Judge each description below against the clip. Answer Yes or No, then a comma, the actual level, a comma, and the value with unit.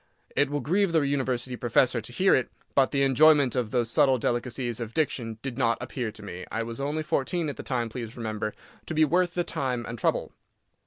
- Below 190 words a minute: No, fast, 205 wpm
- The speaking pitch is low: Yes, low, 130 Hz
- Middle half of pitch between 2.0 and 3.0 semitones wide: No, average, 3.8 semitones